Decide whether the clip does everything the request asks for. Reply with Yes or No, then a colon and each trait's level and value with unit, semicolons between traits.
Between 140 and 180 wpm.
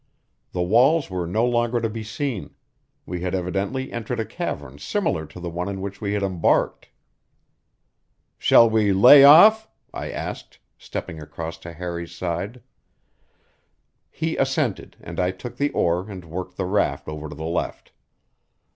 Yes: average, 155 wpm